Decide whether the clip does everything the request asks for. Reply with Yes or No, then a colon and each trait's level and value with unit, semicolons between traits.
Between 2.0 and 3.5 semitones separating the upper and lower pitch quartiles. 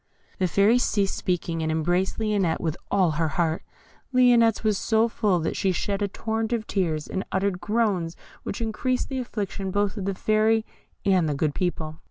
No: average, 4.2 semitones